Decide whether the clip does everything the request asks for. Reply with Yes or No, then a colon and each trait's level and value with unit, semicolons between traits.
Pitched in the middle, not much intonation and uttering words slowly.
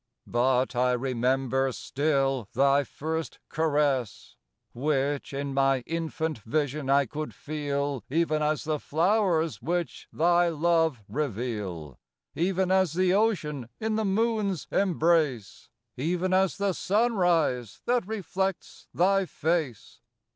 No: medium, 155 Hz; average, 4.9 semitones; slow, 115 wpm